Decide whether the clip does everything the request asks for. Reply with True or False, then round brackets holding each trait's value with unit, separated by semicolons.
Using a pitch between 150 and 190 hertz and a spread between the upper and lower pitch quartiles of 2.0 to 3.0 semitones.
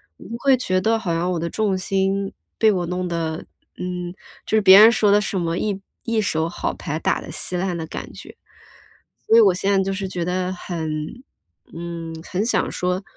True (185 Hz; 2.7 semitones)